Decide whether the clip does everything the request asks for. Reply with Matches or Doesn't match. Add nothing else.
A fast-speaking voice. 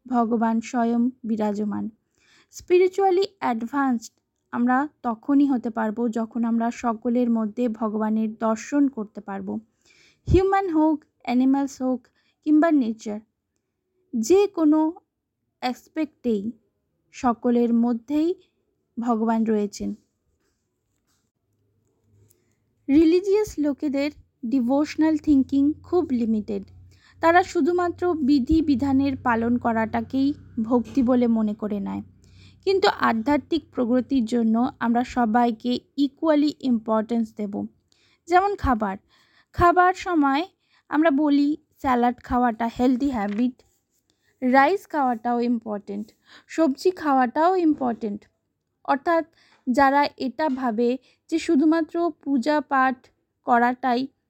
Doesn't match